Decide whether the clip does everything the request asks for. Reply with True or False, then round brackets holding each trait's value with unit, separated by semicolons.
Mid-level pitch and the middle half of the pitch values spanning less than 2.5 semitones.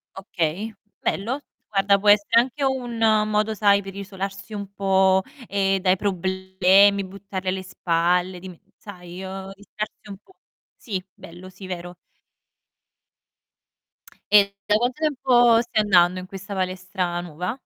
False (195 Hz; 2.1 semitones)